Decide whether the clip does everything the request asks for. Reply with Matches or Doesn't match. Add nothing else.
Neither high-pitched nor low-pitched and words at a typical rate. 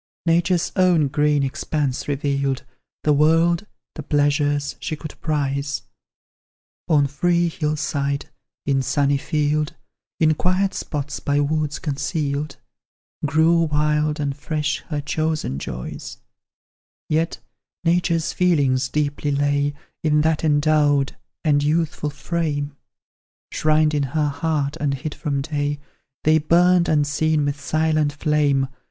Doesn't match